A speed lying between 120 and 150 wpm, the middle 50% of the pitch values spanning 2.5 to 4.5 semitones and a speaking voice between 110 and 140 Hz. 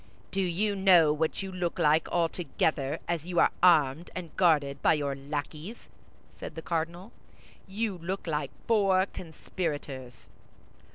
No: average, 145 wpm; average, 3.7 semitones; medium, 170 Hz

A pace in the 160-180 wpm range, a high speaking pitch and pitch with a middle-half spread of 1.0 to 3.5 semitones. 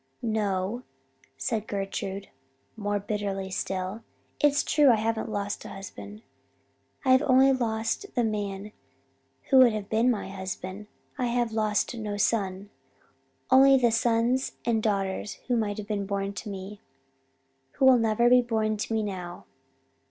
No: average, 150 wpm; high, 215 Hz; average, 3.0 semitones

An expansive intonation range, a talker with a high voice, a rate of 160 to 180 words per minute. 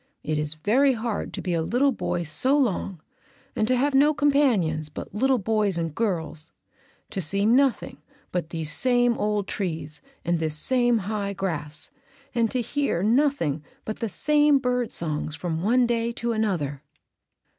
Yes: wide, 7.2 semitones; high, 210 Hz; average, 165 wpm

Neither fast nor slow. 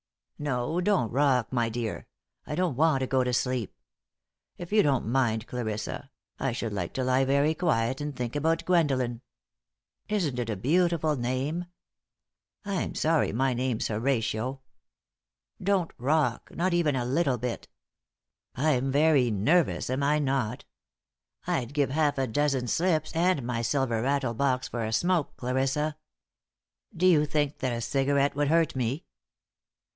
Yes: average, 150 wpm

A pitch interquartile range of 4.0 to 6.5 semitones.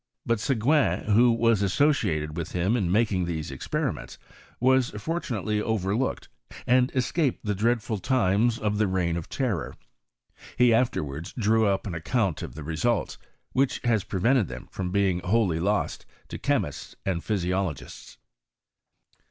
Yes: average, 4.8 semitones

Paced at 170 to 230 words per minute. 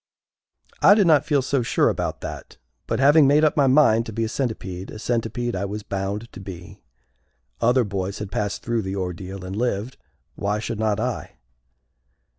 Yes: average, 185 wpm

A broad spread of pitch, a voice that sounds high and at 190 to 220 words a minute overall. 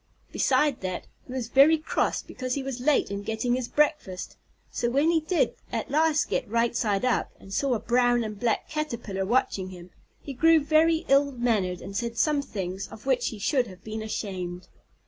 Yes: wide, 5.7 semitones; high, 240 Hz; average, 195 wpm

